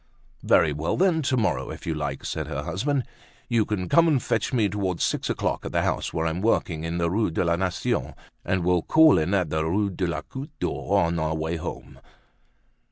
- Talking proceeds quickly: Yes, fast, 220 wpm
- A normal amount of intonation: No, wide, 5.7 semitones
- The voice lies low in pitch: Yes, very low, 90 Hz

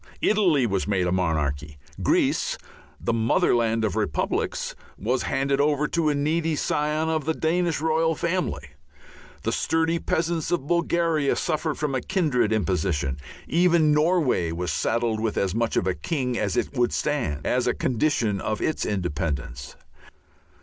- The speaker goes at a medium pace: Yes, average, 150 wpm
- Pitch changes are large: Yes, wide, 7.9 semitones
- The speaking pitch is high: No, low, 135 Hz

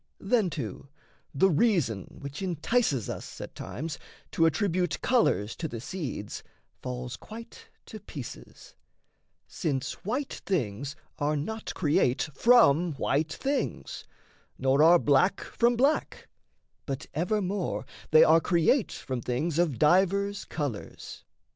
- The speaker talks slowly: Yes, slow, 120 wpm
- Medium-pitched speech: Yes, medium, 160 Hz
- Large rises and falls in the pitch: Yes, wide, 6.3 semitones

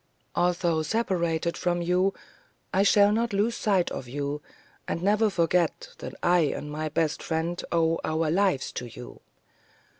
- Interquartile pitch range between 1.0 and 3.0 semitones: No, average, 3.6 semitones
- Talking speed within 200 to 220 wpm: No, average, 150 wpm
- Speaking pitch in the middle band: Yes, medium, 170 Hz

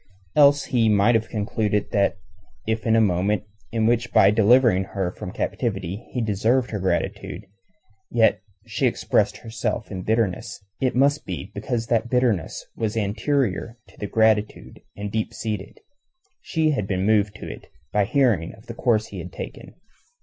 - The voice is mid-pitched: No, low, 110 Hz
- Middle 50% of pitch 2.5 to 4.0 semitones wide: Yes, average, 2.9 semitones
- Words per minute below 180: Yes, average, 165 wpm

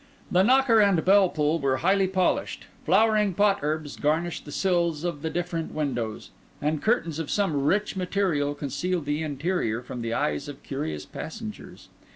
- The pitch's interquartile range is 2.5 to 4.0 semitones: No, average, 4.8 semitones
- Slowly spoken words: No, average, 165 wpm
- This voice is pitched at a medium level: Yes, medium, 165 Hz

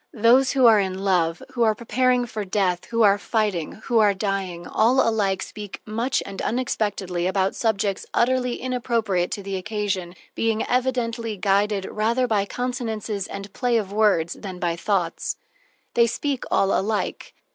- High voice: Yes, high, 210 Hz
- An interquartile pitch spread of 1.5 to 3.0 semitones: No, average, 3.4 semitones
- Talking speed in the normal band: Yes, average, 155 wpm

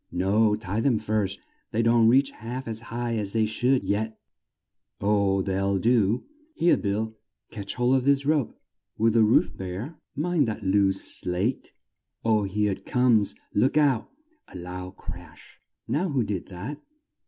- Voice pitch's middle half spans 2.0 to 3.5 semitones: No, average, 3.9 semitones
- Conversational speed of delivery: Yes, average, 155 wpm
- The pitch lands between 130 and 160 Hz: No, low, 110 Hz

